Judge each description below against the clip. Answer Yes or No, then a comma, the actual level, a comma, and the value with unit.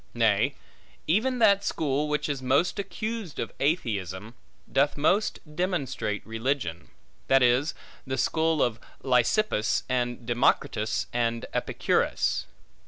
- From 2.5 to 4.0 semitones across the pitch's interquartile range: No, wide, 5.5 semitones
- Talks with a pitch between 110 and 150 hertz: Yes, low, 135 Hz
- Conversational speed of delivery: No, slow, 110 wpm